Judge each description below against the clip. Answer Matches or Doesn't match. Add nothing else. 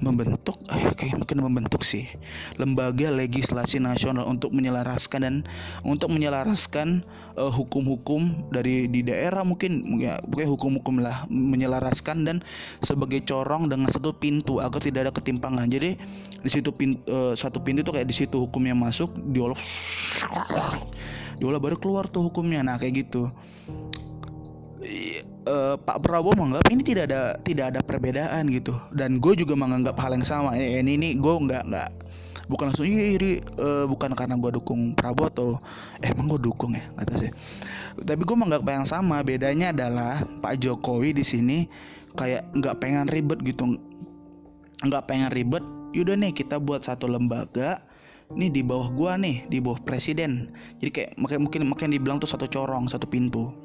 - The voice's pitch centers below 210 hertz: Matches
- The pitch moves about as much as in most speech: Matches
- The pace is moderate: Doesn't match